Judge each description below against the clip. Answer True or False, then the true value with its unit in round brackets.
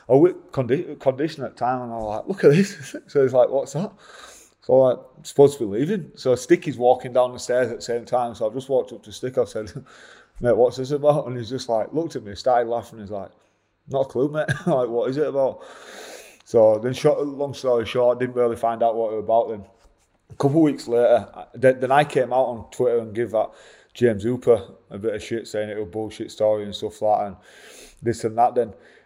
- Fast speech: True (250 wpm)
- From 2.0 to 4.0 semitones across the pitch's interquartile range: True (3.5 semitones)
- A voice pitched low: True (125 Hz)